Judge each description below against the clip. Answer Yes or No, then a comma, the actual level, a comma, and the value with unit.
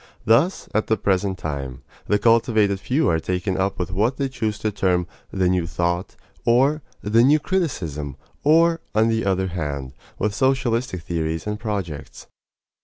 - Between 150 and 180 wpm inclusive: Yes, average, 160 wpm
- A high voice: No, low, 100 Hz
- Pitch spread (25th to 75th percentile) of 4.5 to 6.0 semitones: Yes, average, 5.0 semitones